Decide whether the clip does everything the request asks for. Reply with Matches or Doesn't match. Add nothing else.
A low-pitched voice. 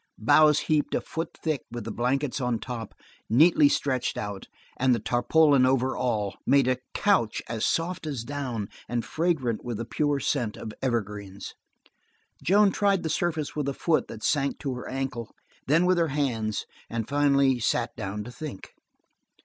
Matches